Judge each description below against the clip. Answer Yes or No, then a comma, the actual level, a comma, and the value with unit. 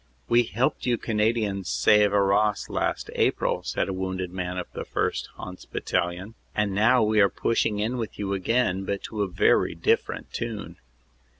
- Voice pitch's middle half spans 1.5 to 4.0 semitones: Yes, average, 2.8 semitones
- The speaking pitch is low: Yes, low, 105 Hz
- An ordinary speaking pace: Yes, average, 170 wpm